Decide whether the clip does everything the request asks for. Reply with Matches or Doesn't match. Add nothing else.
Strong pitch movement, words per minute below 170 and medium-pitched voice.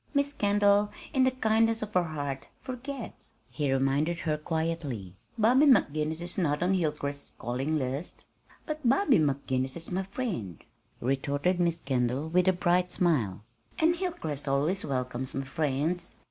Matches